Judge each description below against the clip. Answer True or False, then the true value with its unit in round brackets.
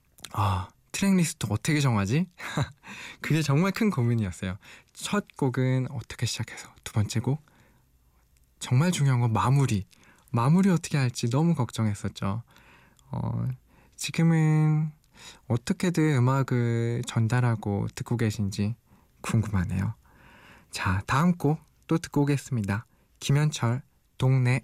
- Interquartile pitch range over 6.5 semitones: False (5.9 semitones)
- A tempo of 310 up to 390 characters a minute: False (250 characters per minute)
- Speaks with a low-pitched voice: True (125 Hz)